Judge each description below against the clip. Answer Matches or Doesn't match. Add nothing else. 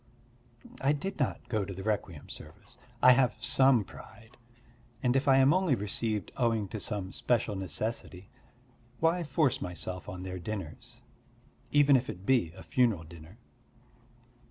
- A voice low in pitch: Matches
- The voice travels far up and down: Matches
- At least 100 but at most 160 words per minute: Matches